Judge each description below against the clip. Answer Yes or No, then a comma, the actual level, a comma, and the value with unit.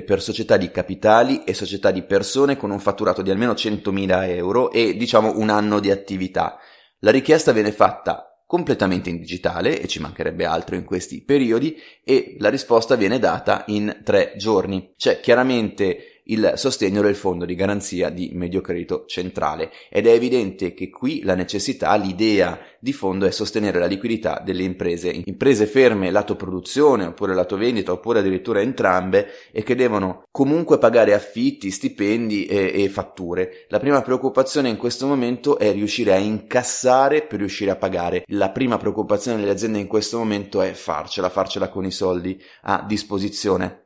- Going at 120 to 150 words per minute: No, average, 165 wpm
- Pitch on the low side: Yes, low, 105 Hz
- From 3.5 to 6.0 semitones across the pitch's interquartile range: Yes, average, 4.6 semitones